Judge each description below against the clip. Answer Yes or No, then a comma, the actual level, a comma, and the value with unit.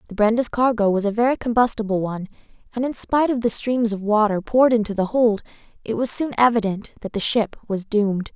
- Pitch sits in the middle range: No, high, 220 Hz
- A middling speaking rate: No, fast, 210 wpm